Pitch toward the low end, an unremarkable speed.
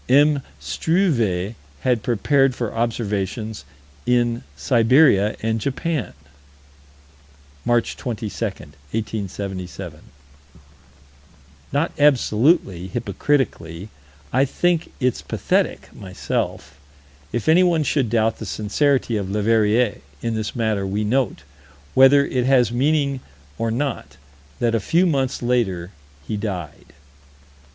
No: low, 115 Hz; slow, 100 wpm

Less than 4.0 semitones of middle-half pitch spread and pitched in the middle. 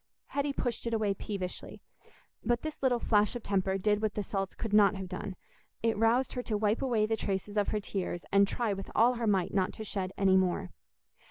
No: average, 2.9 semitones; high, 210 Hz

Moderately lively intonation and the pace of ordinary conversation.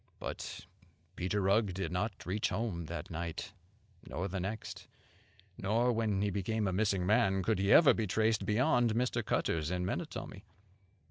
Yes: average, 3.3 semitones; average, 155 wpm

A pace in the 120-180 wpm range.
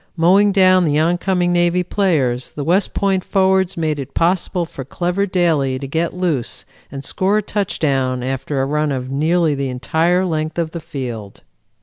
Yes: average, 170 wpm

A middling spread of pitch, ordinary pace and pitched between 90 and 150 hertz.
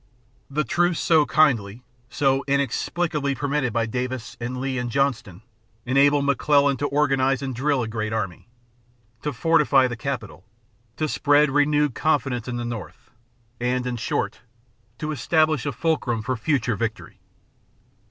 Yes: average, 3.3 semitones; average, 145 wpm; low, 135 Hz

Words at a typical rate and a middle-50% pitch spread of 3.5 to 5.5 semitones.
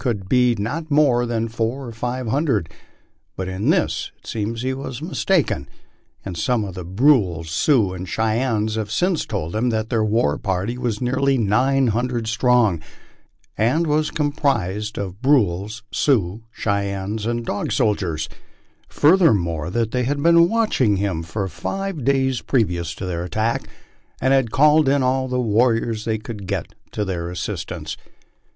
Yes: average, 160 wpm; average, 4.8 semitones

